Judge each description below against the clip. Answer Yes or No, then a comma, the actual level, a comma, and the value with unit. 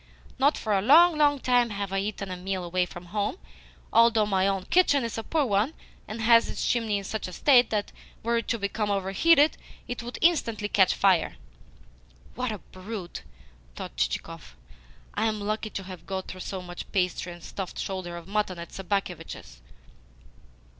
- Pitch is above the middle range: Yes, high, 205 Hz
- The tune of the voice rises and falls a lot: No, average, 3.9 semitones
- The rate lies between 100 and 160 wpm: No, average, 180 wpm